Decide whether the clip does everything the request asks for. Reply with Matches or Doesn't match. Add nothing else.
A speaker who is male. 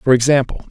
Matches